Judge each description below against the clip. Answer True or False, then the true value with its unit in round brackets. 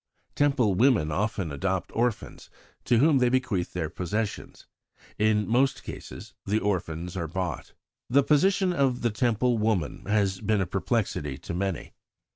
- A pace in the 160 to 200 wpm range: False (145 wpm)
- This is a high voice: False (105 Hz)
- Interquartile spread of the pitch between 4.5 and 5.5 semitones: True (5.2 semitones)